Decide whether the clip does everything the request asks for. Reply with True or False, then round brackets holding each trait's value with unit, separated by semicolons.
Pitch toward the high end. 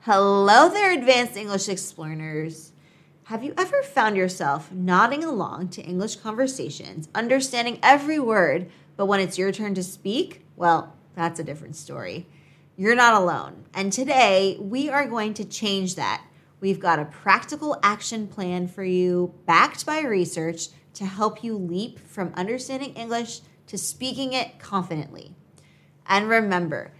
True (195 Hz)